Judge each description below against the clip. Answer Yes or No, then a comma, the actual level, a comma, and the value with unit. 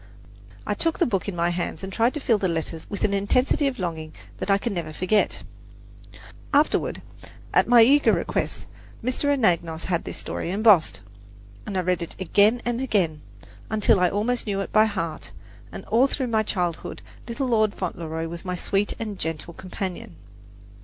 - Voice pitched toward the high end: Yes, high, 200 Hz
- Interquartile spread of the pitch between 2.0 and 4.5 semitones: No, average, 5.0 semitones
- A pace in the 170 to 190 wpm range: Yes, average, 180 wpm